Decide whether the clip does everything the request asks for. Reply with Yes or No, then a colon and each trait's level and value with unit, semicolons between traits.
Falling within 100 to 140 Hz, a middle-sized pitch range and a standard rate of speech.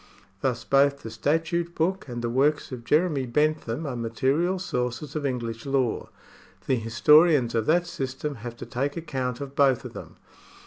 Yes: low, 135 Hz; average, 4.2 semitones; average, 170 wpm